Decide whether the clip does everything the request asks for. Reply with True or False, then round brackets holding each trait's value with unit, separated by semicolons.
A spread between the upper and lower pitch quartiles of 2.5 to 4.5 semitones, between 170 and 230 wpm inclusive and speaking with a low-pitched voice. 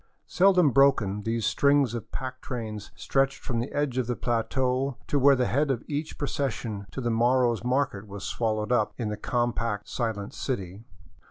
True (3.5 semitones; 180 wpm; 120 Hz)